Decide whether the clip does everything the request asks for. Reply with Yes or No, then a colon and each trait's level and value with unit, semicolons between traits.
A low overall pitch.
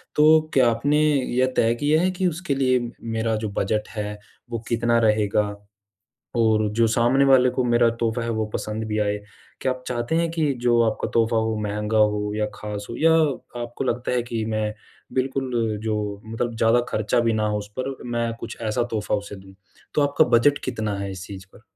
Yes: low, 115 Hz